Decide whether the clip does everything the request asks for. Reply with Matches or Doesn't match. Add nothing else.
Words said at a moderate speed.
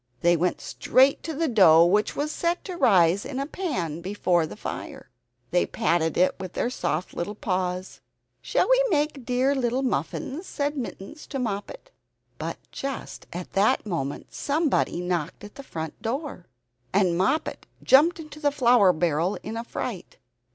Matches